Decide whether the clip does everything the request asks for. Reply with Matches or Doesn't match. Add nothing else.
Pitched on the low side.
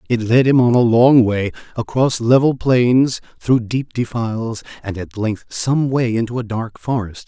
Matches